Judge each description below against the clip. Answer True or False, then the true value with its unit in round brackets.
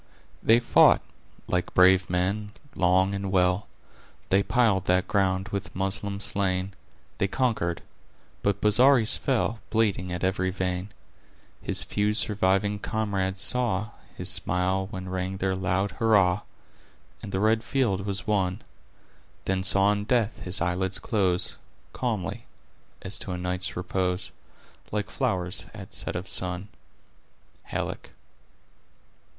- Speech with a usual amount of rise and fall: False (2.1 semitones)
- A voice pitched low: True (95 Hz)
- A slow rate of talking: True (125 wpm)